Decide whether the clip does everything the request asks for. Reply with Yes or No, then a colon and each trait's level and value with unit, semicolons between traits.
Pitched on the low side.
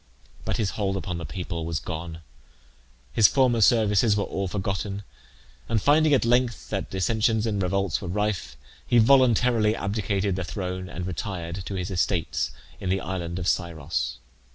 Yes: very low, 95 Hz